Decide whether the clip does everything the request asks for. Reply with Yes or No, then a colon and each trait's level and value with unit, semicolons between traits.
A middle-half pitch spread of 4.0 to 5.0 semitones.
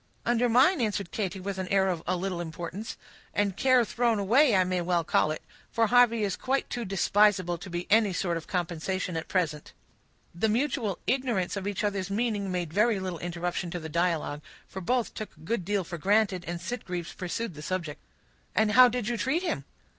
Yes: average, 4.3 semitones